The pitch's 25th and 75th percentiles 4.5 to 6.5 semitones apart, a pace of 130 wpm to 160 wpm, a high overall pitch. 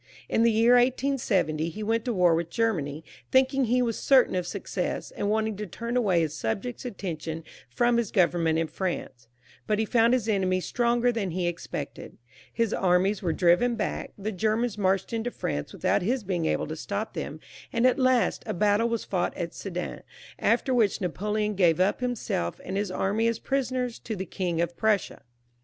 No: average, 4.8 semitones; average, 190 wpm; high, 210 Hz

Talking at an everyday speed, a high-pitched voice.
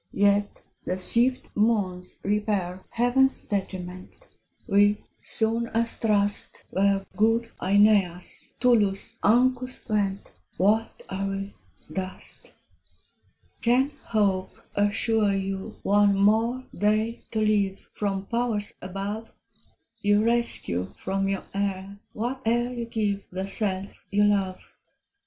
No: slow, 105 wpm; high, 205 Hz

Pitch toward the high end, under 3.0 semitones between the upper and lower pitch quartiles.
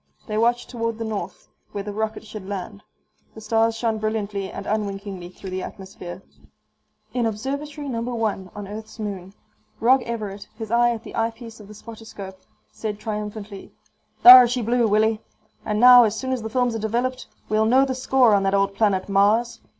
Yes: high, 220 Hz; narrow, 2.6 semitones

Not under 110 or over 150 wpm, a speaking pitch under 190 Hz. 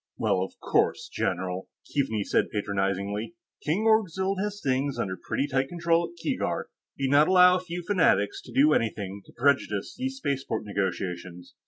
No: average, 160 wpm; low, 135 Hz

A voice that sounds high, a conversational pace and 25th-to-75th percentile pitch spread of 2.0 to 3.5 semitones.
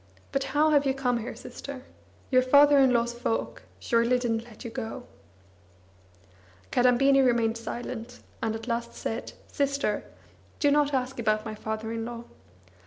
Yes: high, 245 Hz; average, 155 wpm; average, 2.9 semitones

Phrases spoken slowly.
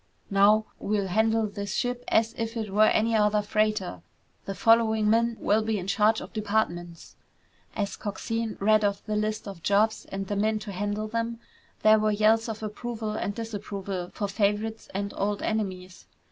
No: average, 175 wpm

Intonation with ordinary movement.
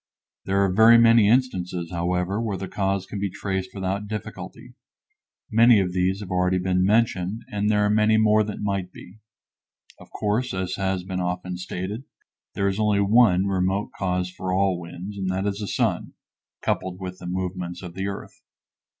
No: narrow, 2.2 semitones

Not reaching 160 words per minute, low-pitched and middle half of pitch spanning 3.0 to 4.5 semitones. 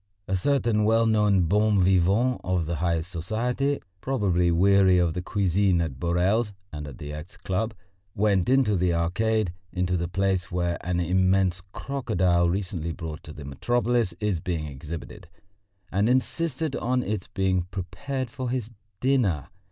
Yes: average, 150 wpm; very low, 95 Hz; average, 4.2 semitones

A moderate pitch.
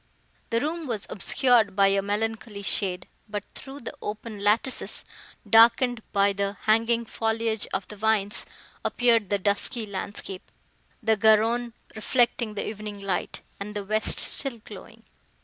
No: high, 215 Hz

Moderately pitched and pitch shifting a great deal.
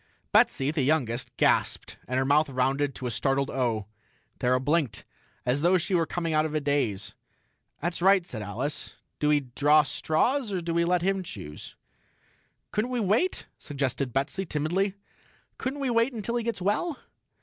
Yes: medium, 155 Hz; wide, 6.2 semitones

